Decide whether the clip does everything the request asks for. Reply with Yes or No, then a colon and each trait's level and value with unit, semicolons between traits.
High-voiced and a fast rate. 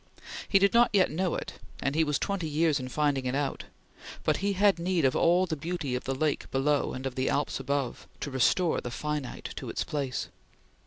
No: medium, 150 Hz; fast, 215 wpm